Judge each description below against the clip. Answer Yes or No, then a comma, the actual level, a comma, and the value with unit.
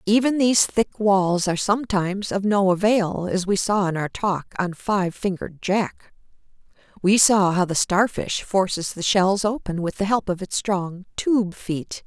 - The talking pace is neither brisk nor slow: Yes, average, 180 wpm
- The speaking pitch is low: No, high, 195 Hz